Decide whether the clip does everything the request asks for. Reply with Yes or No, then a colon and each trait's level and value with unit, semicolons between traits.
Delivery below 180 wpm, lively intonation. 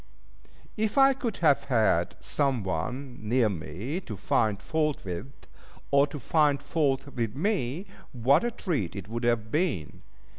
Yes: average, 155 wpm; wide, 6.3 semitones